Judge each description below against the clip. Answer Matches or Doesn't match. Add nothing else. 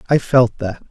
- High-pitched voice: Doesn't match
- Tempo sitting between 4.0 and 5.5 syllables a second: Matches